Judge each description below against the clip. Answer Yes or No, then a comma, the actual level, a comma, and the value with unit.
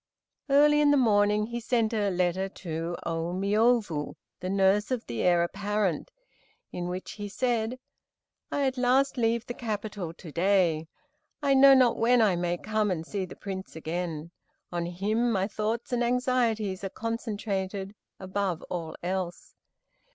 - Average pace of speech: Yes, average, 155 wpm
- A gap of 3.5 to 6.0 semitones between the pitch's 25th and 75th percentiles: Yes, average, 4.6 semitones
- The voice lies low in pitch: No, high, 205 Hz